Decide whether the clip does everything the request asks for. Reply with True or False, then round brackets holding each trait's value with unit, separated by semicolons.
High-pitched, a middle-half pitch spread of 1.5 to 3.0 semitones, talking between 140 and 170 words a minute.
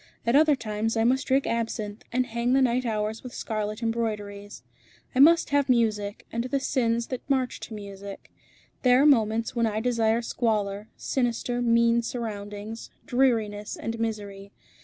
True (230 Hz; 2.7 semitones; 160 wpm)